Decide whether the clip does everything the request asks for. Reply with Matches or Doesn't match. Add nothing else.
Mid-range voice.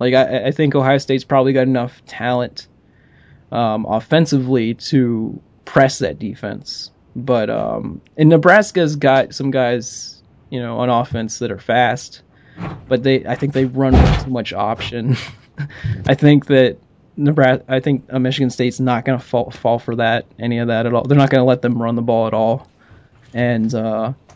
Doesn't match